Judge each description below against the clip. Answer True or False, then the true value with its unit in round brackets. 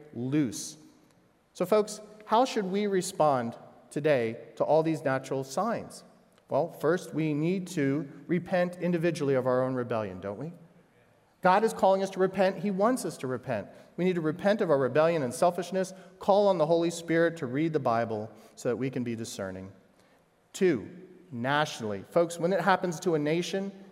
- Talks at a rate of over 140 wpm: True (175 wpm)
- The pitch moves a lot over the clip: True (5.8 semitones)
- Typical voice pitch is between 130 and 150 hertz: False (165 Hz)